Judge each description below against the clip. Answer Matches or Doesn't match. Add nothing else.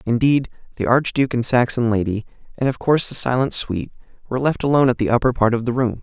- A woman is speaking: Doesn't match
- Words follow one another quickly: Matches